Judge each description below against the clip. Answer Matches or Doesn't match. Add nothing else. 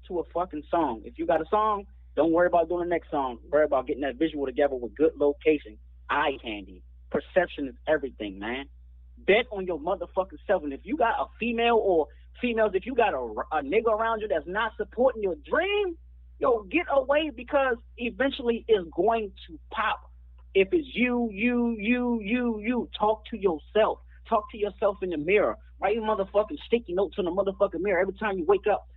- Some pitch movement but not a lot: Doesn't match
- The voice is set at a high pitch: Matches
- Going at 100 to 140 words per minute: Doesn't match